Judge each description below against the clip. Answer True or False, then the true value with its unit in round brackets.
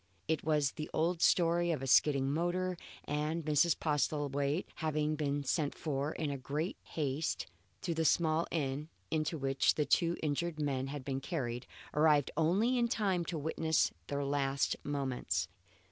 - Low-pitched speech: False (150 Hz)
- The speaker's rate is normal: True (155 wpm)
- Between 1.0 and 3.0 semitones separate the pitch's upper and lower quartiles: True (2.6 semitones)